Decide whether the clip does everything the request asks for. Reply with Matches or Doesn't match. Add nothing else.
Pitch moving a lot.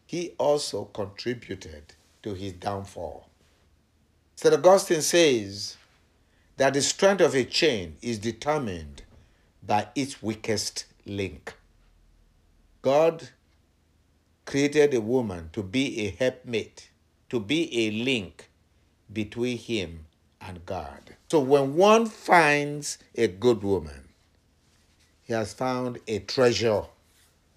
Matches